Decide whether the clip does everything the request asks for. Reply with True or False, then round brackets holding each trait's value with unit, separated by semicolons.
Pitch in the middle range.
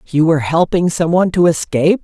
True (170 Hz)